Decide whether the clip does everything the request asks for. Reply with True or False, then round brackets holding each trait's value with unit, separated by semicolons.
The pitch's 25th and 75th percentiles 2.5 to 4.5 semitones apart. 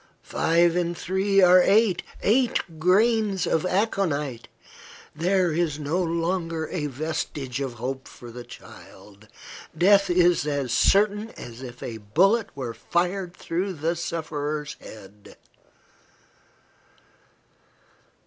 False (4.9 semitones)